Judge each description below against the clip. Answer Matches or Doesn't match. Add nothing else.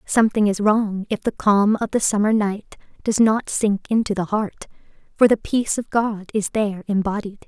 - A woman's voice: Matches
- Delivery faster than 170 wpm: Matches